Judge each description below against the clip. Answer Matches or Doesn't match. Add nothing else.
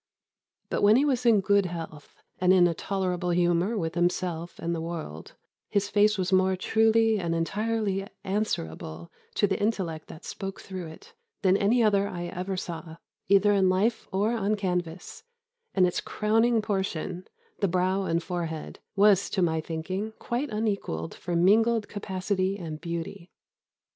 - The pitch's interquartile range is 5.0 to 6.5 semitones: Doesn't match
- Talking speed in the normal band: Matches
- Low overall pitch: Doesn't match